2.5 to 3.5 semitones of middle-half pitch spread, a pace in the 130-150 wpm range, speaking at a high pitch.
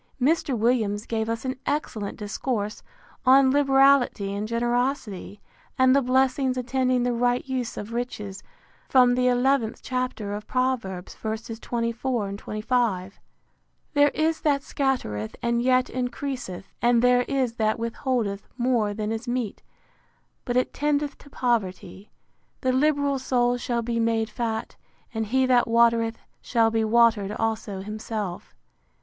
Yes: average, 2.9 semitones; slow, 135 wpm; high, 240 Hz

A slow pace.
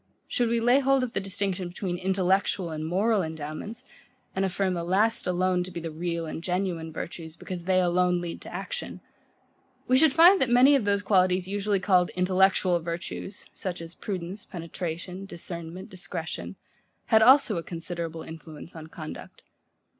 No: average, 165 wpm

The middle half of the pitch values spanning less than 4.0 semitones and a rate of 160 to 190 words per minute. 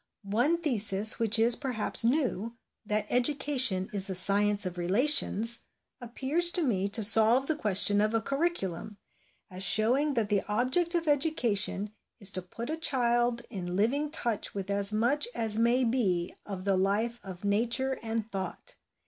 No: average, 4.5 semitones; average, 165 wpm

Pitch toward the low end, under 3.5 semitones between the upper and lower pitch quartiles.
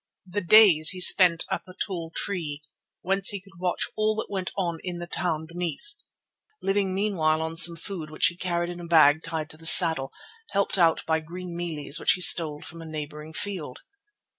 No: medium, 170 Hz; average, 2.7 semitones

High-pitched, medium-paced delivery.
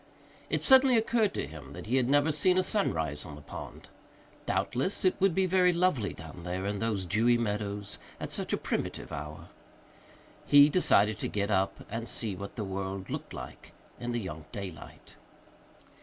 No: low, 105 Hz; average, 180 wpm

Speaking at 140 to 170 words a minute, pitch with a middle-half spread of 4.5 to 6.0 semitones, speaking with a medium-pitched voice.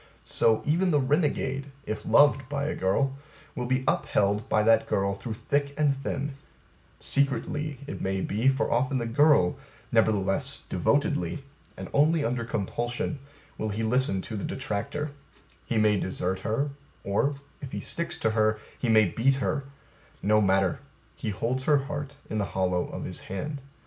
No: average, 165 wpm; average, 5.1 semitones; low, 120 Hz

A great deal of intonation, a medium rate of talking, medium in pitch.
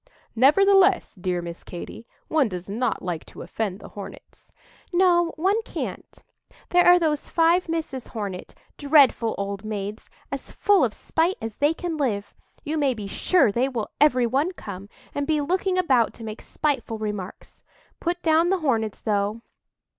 No: wide, 7.9 semitones; average, 155 wpm; very high, 265 Hz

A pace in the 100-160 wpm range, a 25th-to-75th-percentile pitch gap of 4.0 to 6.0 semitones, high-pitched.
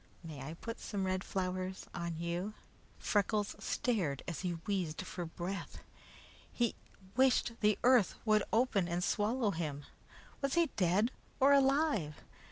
Yes: average, 140 wpm; average, 5.3 semitones; high, 195 Hz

